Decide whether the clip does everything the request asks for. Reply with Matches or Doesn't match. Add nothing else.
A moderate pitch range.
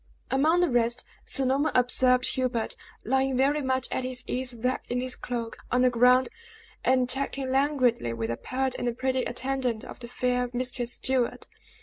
Doesn't match